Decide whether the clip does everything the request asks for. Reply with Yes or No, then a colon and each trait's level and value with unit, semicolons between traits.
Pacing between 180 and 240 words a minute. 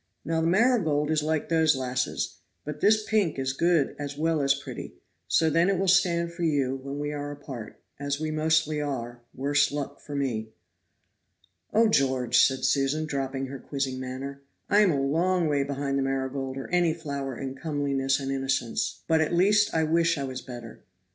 Yes: average, 185 wpm